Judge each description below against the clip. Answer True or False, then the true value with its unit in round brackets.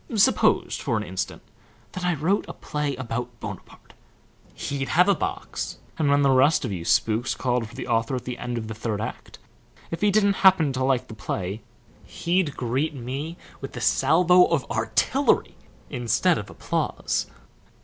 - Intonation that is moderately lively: False (6.3 semitones)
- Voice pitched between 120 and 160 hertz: True (135 Hz)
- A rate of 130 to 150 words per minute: False (175 wpm)